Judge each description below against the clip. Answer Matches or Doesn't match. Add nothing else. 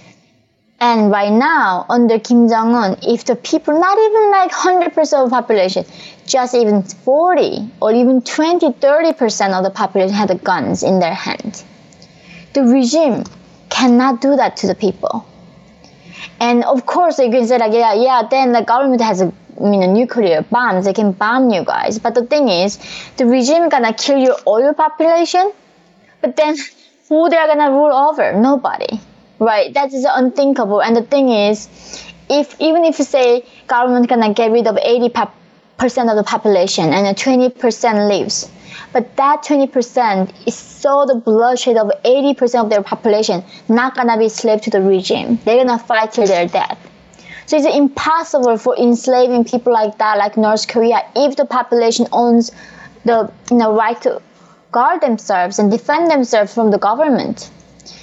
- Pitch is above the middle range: Matches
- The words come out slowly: Doesn't match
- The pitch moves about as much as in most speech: Matches